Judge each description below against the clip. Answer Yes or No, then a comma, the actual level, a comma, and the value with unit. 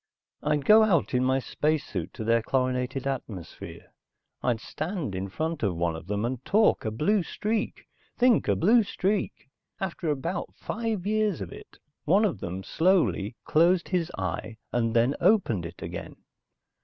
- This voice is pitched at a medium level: Yes, medium, 145 Hz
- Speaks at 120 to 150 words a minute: No, average, 160 wpm